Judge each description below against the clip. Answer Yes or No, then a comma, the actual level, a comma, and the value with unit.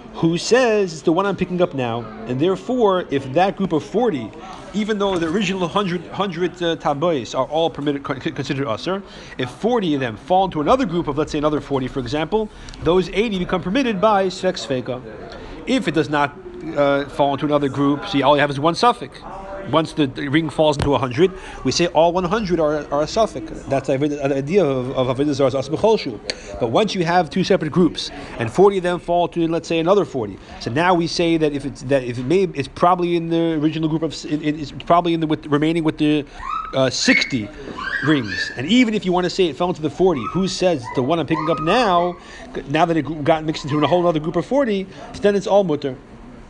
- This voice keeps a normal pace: No, fast, 225 wpm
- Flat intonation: No, average, 4.3 semitones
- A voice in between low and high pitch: Yes, medium, 165 Hz